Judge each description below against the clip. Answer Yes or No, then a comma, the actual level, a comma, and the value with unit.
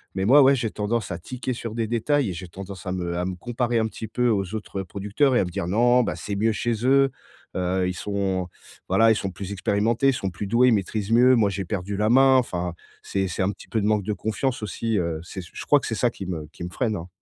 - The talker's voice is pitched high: No, low, 105 Hz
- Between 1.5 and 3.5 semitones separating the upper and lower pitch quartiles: No, average, 4.1 semitones